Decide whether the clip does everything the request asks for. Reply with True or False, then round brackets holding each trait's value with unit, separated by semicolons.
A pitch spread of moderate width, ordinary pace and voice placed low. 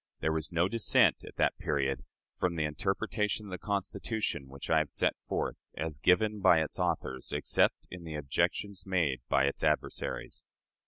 True (4.9 semitones; 170 wpm; 80 Hz)